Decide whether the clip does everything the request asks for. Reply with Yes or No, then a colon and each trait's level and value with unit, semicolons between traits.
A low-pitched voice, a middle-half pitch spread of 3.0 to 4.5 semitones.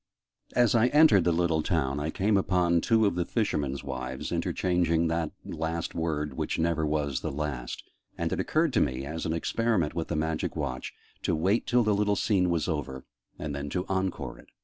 Yes: very low, 80 Hz; average, 4.2 semitones